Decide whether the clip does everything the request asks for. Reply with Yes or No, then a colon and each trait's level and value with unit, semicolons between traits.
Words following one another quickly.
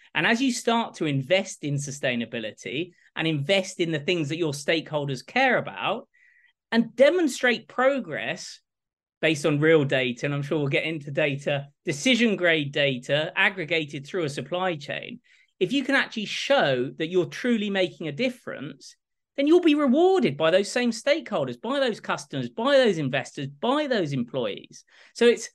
No: average, 165 wpm